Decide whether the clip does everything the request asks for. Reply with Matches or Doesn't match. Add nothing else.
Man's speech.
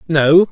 Matches